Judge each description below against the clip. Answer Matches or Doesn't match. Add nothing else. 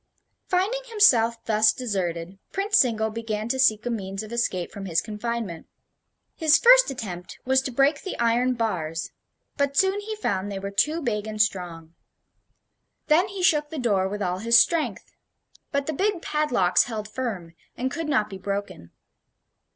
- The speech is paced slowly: Doesn't match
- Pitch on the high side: Matches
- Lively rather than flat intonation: Matches